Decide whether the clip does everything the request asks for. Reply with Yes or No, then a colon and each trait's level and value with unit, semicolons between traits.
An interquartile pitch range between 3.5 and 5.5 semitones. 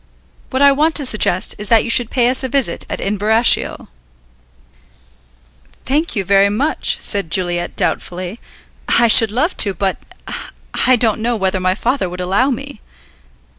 Yes: average, 5.1 semitones